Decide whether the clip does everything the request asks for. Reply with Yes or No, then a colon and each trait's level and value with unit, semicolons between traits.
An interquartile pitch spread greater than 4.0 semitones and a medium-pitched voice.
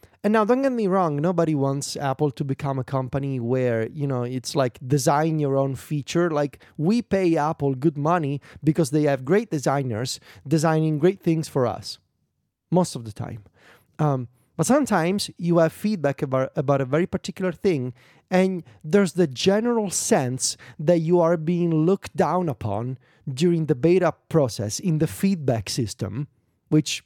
Yes: average, 4.9 semitones; medium, 150 Hz